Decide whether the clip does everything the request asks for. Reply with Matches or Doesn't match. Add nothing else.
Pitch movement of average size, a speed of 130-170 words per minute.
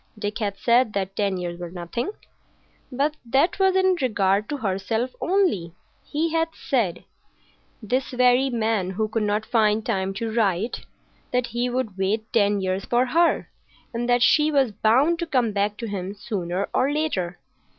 Matches